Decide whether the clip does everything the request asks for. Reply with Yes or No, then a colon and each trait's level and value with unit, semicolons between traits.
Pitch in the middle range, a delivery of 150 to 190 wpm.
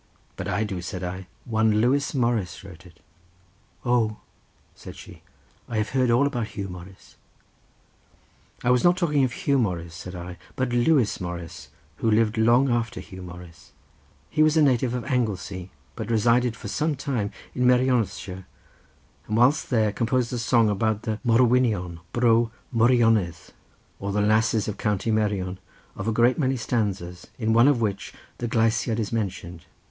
No: low, 110 Hz; average, 165 wpm